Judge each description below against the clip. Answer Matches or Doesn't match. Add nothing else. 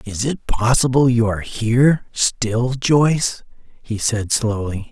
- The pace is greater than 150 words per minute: Doesn't match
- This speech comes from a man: Matches